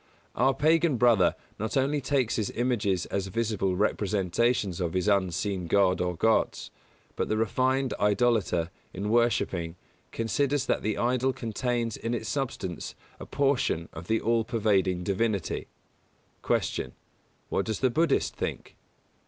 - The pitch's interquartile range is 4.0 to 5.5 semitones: Yes, average, 4.4 semitones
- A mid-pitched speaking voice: No, low, 110 Hz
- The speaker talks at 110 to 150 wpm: Yes, average, 140 wpm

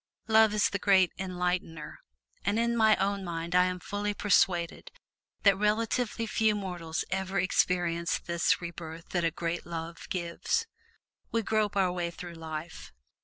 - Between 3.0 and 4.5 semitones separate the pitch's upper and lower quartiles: Yes, average, 3.4 semitones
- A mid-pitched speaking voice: Yes, medium, 180 Hz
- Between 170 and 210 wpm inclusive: No, average, 150 wpm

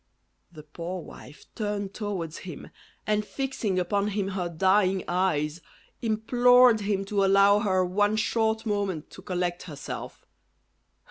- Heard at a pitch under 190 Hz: No, high, 195 Hz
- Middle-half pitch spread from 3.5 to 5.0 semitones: No, average, 2.8 semitones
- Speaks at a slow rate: Yes, slow, 130 wpm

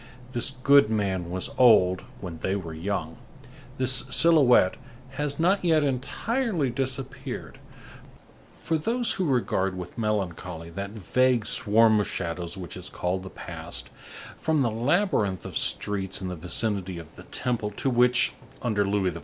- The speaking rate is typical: Yes, average, 145 wpm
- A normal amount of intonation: No, wide, 6.2 semitones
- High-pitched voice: No, low, 110 Hz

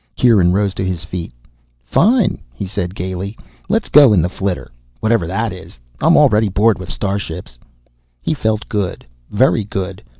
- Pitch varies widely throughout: No, average, 3.4 semitones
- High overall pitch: No, low, 100 Hz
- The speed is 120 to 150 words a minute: No, average, 170 wpm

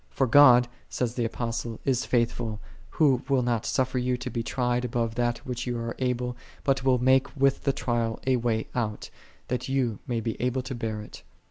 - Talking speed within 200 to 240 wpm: Yes, fast, 205 wpm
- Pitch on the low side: Yes, low, 125 Hz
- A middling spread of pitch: No, narrow, 1.9 semitones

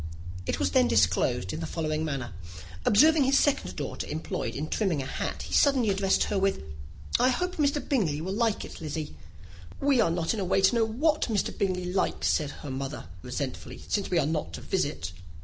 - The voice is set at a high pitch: No, medium, 180 Hz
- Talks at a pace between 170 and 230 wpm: Yes, average, 200 wpm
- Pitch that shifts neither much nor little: No, wide, 8.1 semitones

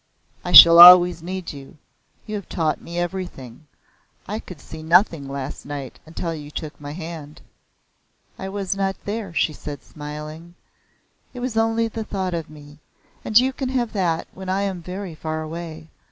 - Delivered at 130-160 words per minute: No, average, 170 wpm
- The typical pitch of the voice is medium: Yes, medium, 170 Hz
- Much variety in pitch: No, average, 3.9 semitones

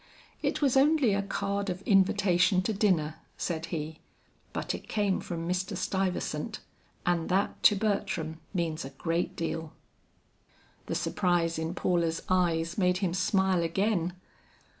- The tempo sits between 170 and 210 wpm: No, average, 140 wpm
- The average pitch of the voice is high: No, medium, 180 Hz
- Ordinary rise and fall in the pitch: Yes, average, 3.0 semitones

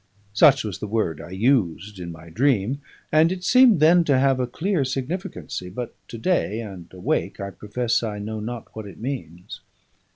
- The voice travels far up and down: Yes, wide, 6.1 semitones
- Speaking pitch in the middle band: No, low, 115 Hz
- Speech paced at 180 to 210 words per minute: Yes, average, 185 wpm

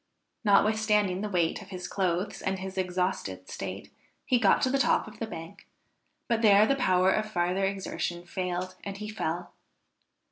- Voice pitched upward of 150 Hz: Yes, high, 190 Hz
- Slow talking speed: No, average, 170 wpm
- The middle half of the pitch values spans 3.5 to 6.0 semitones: No, average, 2.9 semitones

